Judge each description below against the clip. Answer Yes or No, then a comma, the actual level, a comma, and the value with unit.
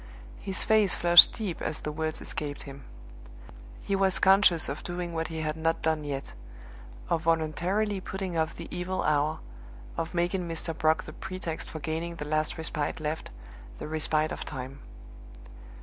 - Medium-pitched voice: Yes, medium, 160 Hz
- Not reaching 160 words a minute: No, average, 165 wpm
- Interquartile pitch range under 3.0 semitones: Yes, narrow, 2.5 semitones